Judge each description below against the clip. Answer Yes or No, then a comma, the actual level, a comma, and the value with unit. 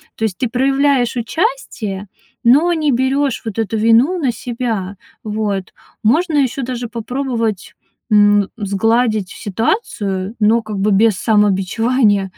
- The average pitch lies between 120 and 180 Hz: No, high, 225 Hz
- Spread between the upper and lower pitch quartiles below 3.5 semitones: No, average, 3.9 semitones